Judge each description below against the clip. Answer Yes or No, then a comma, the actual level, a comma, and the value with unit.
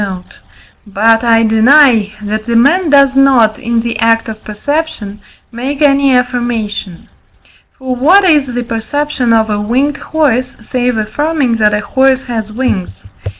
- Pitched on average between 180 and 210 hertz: No, high, 240 Hz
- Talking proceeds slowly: No, average, 150 wpm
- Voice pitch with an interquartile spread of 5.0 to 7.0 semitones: No, average, 4.0 semitones